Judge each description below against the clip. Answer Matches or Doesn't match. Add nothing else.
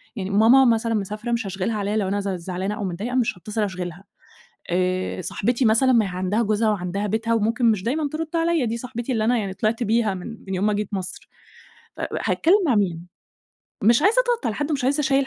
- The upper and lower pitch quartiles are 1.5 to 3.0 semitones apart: Doesn't match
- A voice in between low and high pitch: Doesn't match